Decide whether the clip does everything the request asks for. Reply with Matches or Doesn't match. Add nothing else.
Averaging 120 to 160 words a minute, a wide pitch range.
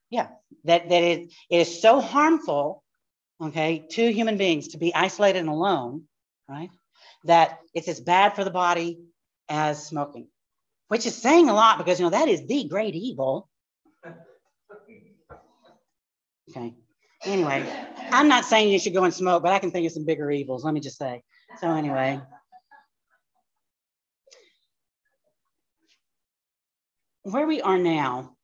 Matches